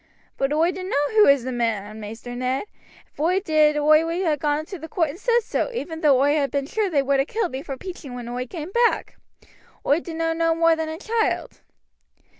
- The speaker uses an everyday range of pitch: Yes, average, 4.3 semitones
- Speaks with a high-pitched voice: Yes, very high, 310 Hz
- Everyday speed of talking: No, fast, 225 wpm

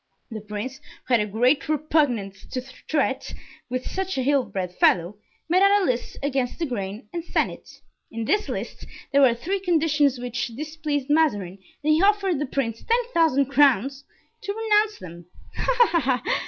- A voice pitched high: Yes, very high, 275 Hz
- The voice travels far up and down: Yes, wide, 5.8 semitones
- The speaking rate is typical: Yes, average, 180 wpm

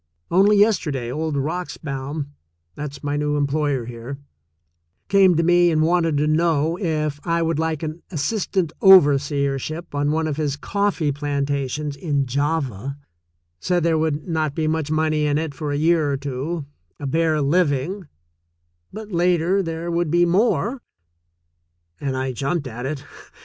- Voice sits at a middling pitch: Yes, medium, 150 Hz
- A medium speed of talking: Yes, average, 160 wpm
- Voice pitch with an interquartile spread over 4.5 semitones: No, average, 3.1 semitones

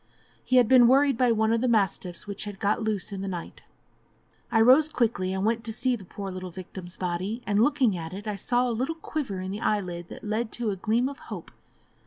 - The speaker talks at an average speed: No, fast, 235 wpm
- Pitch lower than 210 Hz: No, high, 215 Hz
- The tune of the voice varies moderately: Yes, average, 4.2 semitones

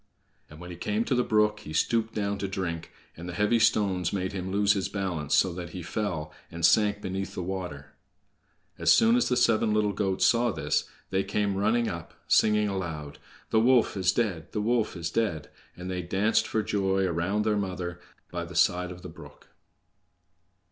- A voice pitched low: Yes, very low, 95 Hz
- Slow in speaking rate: No, average, 195 wpm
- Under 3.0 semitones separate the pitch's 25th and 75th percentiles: No, average, 3.3 semitones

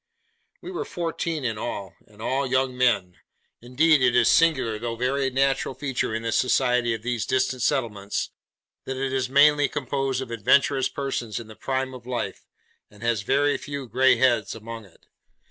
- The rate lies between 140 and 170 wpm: No, average, 180 wpm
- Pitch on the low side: Yes, low, 130 Hz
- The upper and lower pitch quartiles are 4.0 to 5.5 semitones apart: No, average, 2.9 semitones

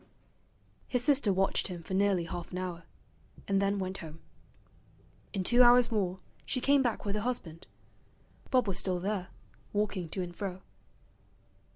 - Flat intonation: No, average, 3.8 semitones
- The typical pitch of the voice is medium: No, high, 195 Hz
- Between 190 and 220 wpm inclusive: No, average, 160 wpm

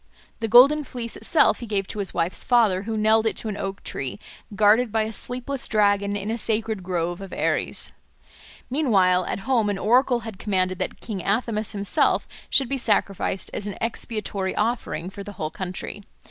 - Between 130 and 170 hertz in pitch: No, high, 210 Hz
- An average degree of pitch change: Yes, average, 3.0 semitones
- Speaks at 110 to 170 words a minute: No, average, 185 wpm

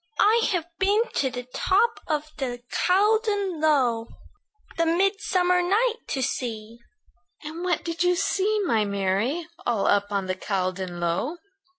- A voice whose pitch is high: Yes, very high, 310 Hz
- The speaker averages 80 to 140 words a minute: Yes, slow, 135 wpm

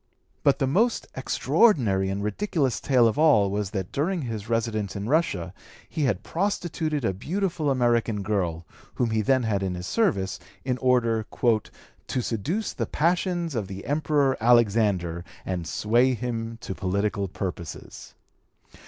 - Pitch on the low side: Yes, low, 115 Hz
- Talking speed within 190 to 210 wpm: No, average, 155 wpm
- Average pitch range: No, wide, 6.5 semitones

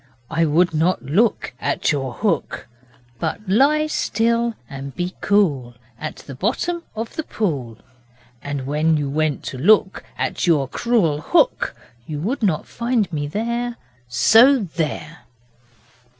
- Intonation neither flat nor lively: No, wide, 7.6 semitones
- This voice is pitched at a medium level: Yes, medium, 170 Hz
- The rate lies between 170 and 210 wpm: No, slow, 135 wpm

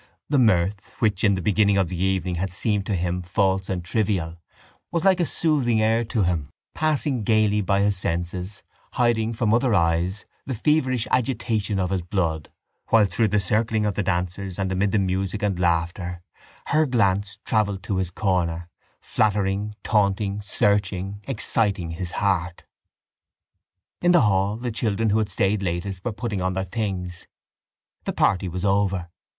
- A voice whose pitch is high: No, low, 100 Hz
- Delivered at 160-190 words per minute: Yes, average, 165 wpm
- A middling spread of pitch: Yes, average, 3.0 semitones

